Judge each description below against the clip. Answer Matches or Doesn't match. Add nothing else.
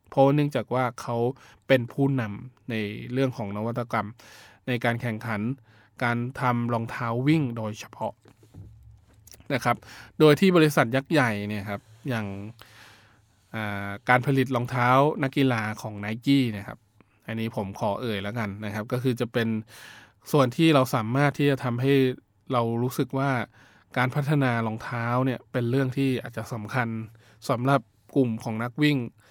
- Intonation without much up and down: Doesn't match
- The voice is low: Matches